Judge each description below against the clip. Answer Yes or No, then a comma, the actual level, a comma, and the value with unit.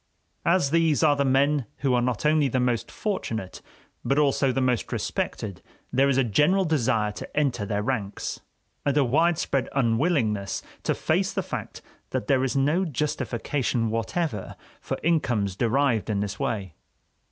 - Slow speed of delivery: No, average, 160 wpm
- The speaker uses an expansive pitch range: No, average, 4.7 semitones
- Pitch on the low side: Yes, low, 130 Hz